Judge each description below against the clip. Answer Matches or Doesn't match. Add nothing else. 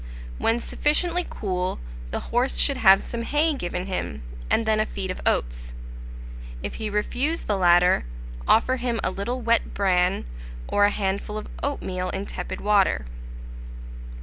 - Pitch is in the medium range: Doesn't match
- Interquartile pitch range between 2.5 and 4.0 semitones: Doesn't match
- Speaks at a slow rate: Doesn't match